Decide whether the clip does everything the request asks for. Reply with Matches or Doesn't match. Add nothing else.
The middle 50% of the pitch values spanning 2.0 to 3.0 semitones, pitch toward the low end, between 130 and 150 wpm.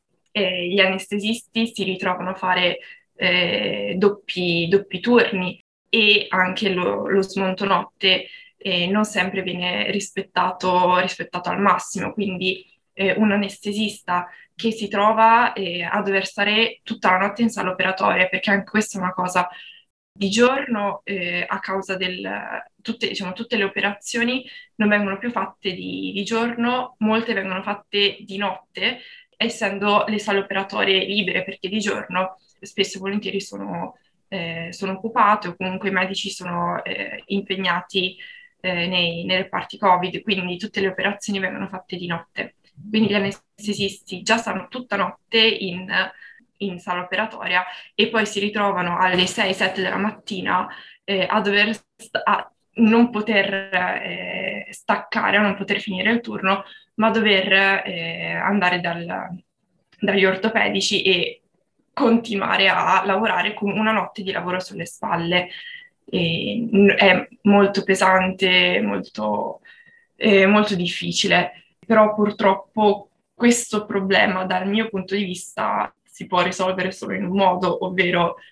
Doesn't match